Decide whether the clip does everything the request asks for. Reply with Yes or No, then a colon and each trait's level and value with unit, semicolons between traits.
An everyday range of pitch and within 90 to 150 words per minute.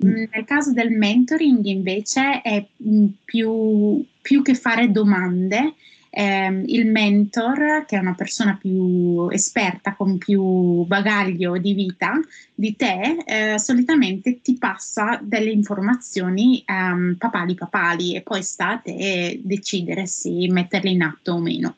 Yes: average, 3.7 semitones; average, 130 wpm